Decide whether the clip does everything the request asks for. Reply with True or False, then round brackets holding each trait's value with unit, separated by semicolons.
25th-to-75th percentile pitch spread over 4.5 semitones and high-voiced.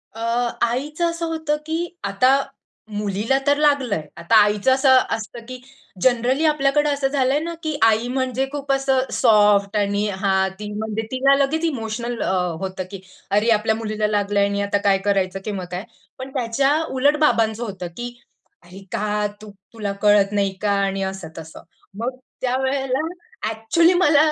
True (4.9 semitones; 230 Hz)